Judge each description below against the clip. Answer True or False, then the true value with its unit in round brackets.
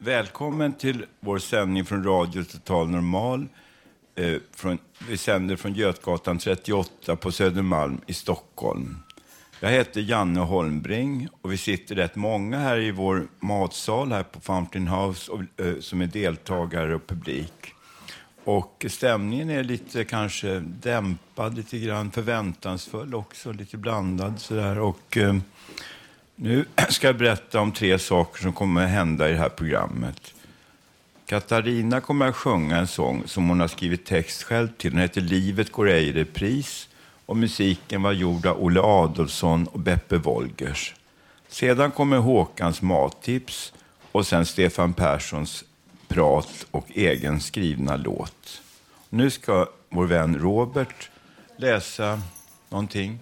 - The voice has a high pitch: False (95 Hz)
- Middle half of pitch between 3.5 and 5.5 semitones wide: True (4.4 semitones)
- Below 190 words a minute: True (140 wpm)